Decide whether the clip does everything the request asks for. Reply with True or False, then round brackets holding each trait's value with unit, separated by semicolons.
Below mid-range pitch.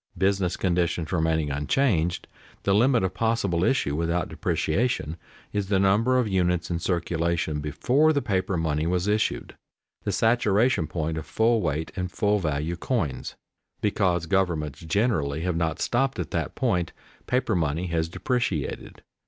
True (90 Hz)